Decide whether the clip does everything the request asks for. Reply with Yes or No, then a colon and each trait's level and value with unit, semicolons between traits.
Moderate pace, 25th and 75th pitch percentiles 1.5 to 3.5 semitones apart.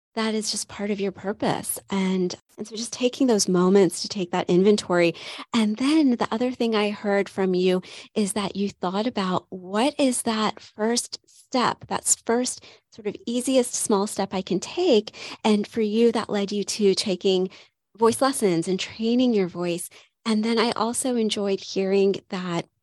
Yes: average, 180 wpm; average, 3.1 semitones